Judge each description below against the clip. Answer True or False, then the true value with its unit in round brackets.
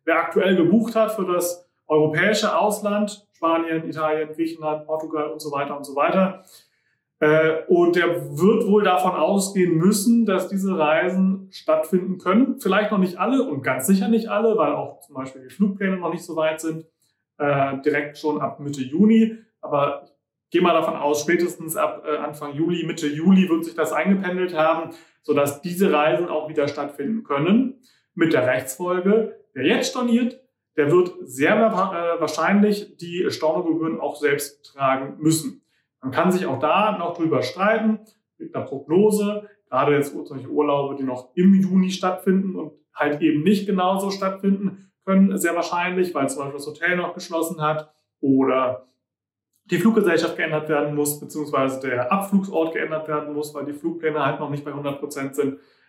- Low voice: False (165 Hz)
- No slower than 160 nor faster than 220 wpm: True (165 wpm)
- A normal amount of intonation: True (4.5 semitones)